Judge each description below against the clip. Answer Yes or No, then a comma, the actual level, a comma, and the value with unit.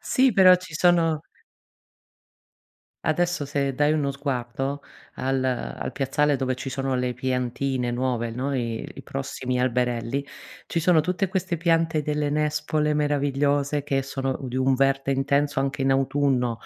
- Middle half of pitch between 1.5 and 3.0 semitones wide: Yes, narrow, 2.5 semitones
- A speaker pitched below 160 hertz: Yes, medium, 140 Hz